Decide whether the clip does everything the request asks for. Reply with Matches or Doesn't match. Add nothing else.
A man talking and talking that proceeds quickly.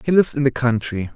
Matches